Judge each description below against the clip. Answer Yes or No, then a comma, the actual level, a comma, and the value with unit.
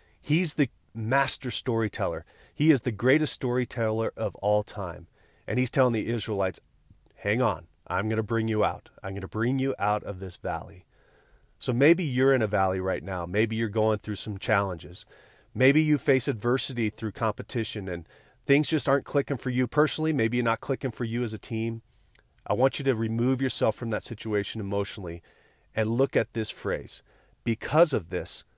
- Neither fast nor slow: Yes, average, 185 wpm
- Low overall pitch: Yes, low, 115 Hz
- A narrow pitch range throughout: No, average, 4.0 semitones